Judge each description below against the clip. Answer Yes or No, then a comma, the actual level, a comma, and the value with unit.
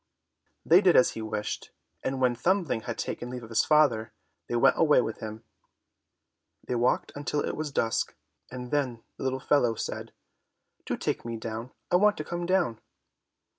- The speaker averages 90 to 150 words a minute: No, average, 175 wpm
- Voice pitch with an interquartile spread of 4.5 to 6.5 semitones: Yes, average, 5.0 semitones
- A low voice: Yes, low, 125 Hz